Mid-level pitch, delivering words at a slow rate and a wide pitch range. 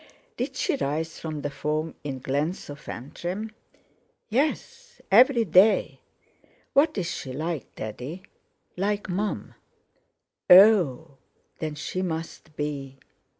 Yes: medium, 165 Hz; slow, 105 wpm; wide, 5.8 semitones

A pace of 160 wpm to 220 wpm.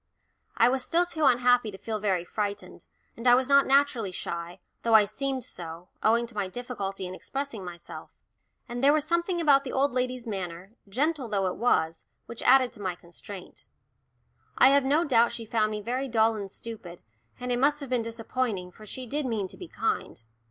Yes: average, 200 wpm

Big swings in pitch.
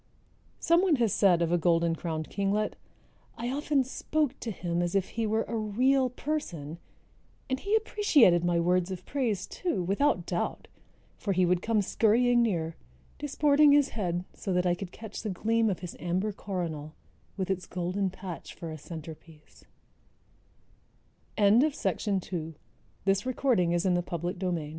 Yes: wide, 5.8 semitones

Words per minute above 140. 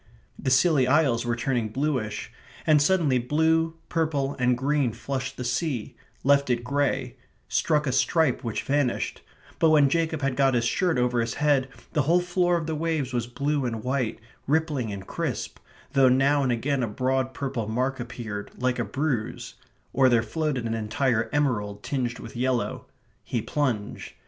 Yes: average, 170 wpm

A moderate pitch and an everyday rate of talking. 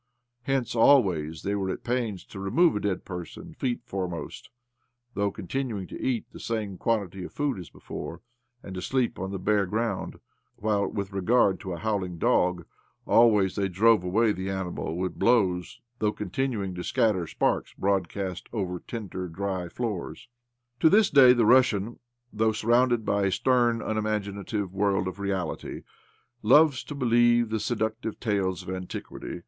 No: low, 105 Hz; average, 170 wpm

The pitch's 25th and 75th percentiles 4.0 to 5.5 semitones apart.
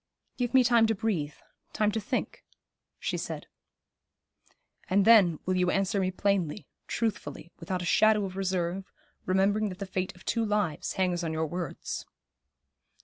No: average, 2.9 semitones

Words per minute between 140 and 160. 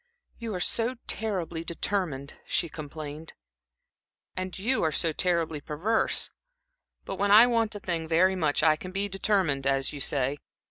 Yes: average, 155 wpm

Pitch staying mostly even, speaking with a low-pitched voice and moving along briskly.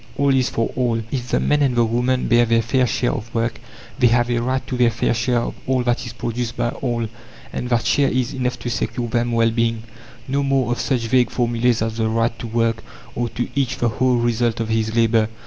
Yes: narrow, 1.5 semitones; low, 120 Hz; fast, 235 wpm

